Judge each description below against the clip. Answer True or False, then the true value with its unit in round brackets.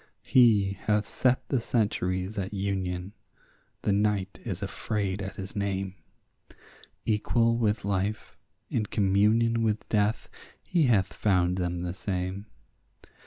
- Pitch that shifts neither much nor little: False (2.3 semitones)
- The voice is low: True (100 Hz)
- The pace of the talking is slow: True (120 wpm)